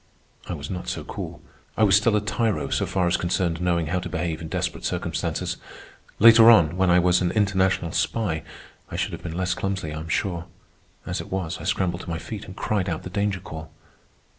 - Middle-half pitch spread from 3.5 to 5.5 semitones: No, average, 2.7 semitones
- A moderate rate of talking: No, fast, 215 wpm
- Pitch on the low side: Yes, very low, 90 Hz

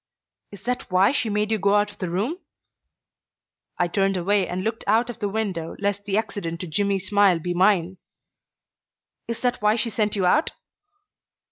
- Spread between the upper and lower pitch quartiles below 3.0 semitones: Yes, narrow, 2.6 semitones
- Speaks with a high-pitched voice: Yes, high, 205 Hz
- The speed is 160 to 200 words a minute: Yes, average, 180 wpm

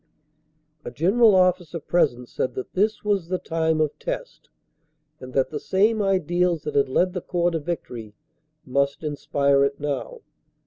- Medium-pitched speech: Yes, medium, 165 Hz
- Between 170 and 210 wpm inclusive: No, average, 155 wpm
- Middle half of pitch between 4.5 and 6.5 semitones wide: Yes, average, 4.8 semitones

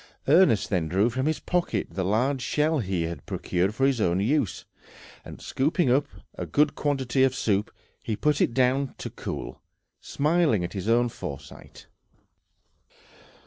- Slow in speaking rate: No, average, 155 wpm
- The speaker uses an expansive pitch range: Yes, wide, 6.4 semitones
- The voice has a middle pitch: No, low, 125 Hz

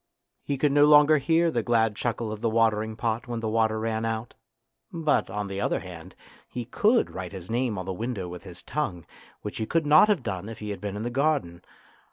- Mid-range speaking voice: No, low, 115 Hz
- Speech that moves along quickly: Yes, fast, 230 wpm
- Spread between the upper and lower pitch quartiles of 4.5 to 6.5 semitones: Yes, average, 5.0 semitones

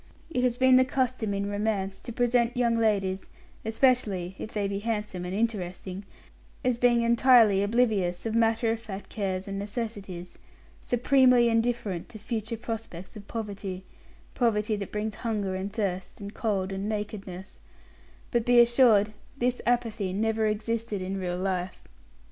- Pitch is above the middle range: Yes, high, 215 Hz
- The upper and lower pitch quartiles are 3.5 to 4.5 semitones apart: No, average, 3.1 semitones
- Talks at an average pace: Yes, average, 150 wpm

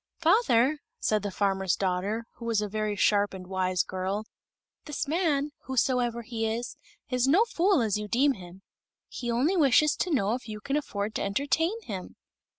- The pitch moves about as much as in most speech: No, wide, 5.8 semitones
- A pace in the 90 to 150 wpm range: No, average, 175 wpm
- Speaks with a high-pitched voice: Yes, high, 230 Hz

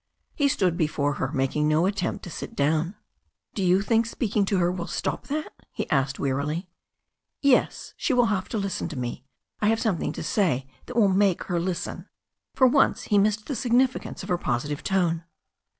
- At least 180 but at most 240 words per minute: Yes, average, 190 wpm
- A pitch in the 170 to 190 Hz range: Yes, medium, 185 Hz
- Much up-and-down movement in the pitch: Yes, wide, 6.1 semitones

